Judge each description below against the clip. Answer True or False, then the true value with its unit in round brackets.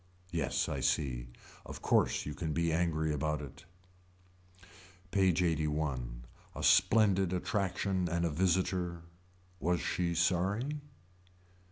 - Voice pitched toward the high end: False (85 Hz)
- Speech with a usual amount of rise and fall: True (3.4 semitones)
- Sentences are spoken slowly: True (115 wpm)